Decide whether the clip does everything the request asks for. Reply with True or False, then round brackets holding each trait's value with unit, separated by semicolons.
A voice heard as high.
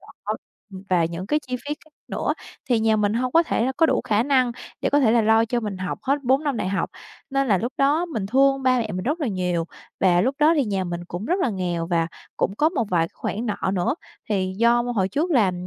True (225 Hz)